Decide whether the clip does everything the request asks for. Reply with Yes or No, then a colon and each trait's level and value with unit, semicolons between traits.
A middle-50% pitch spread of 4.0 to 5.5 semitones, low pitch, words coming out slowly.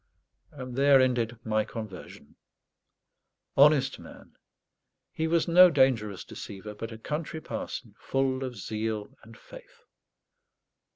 Yes: average, 5.0 semitones; low, 130 Hz; slow, 115 wpm